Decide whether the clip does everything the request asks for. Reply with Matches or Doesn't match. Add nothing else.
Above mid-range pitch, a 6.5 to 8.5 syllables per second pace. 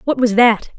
Doesn't match